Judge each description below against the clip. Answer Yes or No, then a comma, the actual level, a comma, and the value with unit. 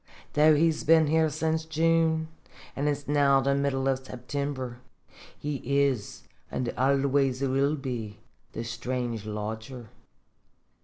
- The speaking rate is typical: No, slow, 120 wpm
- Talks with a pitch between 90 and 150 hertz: Yes, medium, 140 Hz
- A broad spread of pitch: No, average, 2.9 semitones